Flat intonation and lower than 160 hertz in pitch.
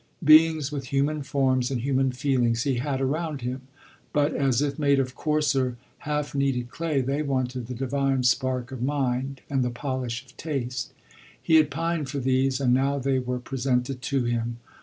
Yes: narrow, 2.1 semitones; low, 135 Hz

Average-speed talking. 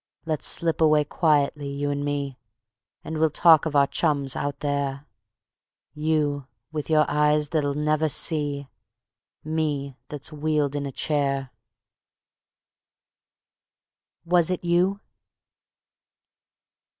No: slow, 110 wpm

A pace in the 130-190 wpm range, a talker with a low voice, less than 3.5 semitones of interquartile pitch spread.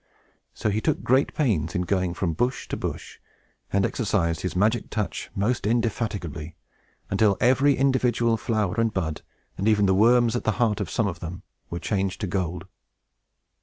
No: average, 170 wpm; low, 105 Hz; average, 4.2 semitones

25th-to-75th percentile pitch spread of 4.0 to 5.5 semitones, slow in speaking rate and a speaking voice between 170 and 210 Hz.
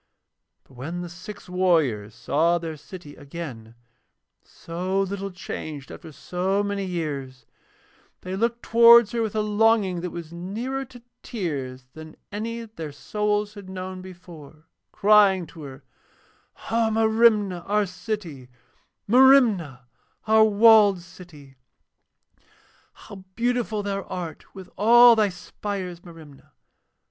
Yes: average, 4.7 semitones; slow, 125 wpm; medium, 185 Hz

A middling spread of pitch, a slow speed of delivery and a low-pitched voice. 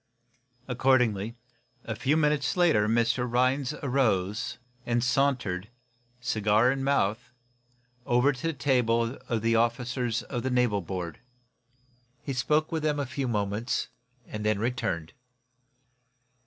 Yes: average, 3.6 semitones; slow, 115 wpm; low, 120 Hz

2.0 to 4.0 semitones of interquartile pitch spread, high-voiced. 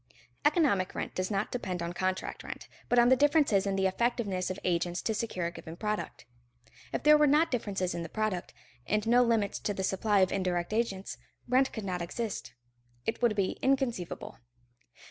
No: average, 4.4 semitones; high, 205 Hz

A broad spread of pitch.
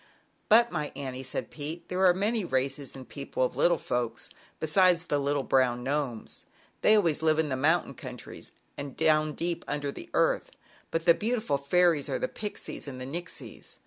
No: average, 4.1 semitones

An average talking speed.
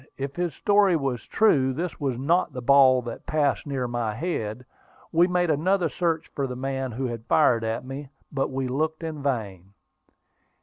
Yes: average, 180 wpm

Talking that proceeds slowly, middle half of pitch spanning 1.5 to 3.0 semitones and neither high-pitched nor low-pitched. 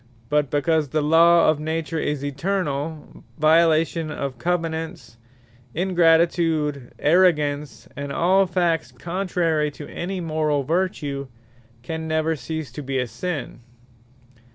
Yes: slow, 110 wpm; narrow, 2.5 semitones; medium, 160 Hz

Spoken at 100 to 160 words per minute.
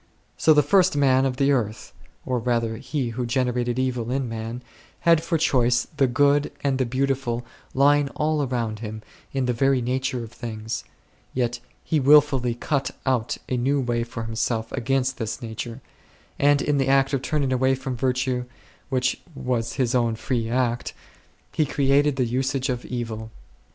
No: average, 170 wpm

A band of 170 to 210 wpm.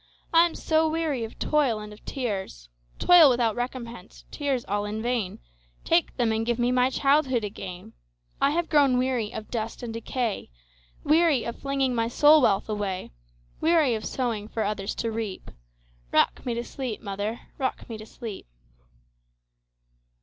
No: average, 140 wpm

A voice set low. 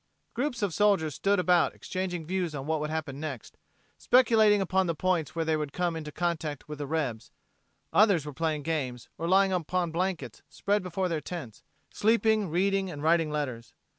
No: medium, 170 Hz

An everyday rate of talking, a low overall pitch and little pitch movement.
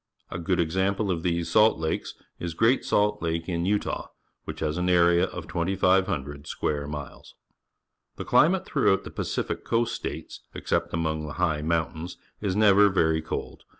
No: average, 155 wpm; very low, 85 Hz; average, 3.6 semitones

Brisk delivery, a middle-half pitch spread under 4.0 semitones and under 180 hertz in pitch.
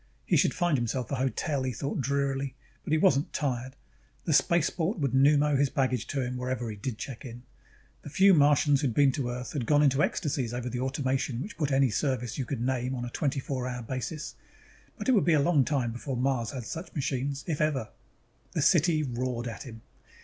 Yes: fast, 215 wpm; average, 2.7 semitones; low, 135 Hz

